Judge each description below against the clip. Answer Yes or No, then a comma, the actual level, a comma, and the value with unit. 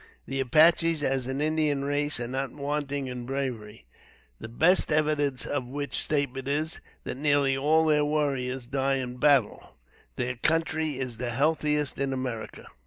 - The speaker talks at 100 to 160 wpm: Yes, average, 155 wpm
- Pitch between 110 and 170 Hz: Yes, medium, 140 Hz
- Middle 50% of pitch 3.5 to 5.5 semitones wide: No, narrow, 2.6 semitones